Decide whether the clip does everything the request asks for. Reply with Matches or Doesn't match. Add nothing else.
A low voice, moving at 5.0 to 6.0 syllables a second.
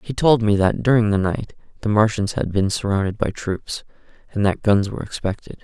Matches